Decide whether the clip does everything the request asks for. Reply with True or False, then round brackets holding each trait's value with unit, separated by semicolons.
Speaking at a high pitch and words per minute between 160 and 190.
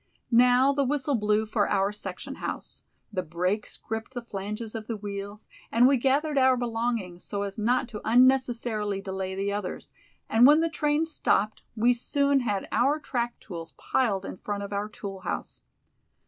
True (220 Hz; 175 wpm)